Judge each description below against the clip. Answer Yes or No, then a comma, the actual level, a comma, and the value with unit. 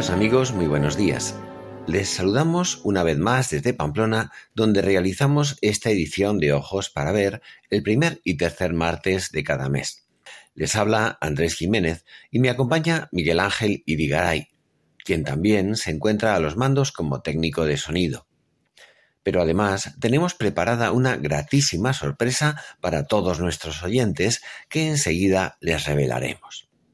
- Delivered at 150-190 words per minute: No, average, 140 wpm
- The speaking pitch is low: Yes, low, 100 Hz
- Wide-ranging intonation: Yes, wide, 6.5 semitones